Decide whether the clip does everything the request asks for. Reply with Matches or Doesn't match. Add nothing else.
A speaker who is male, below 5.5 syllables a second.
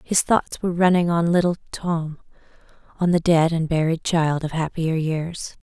Doesn't match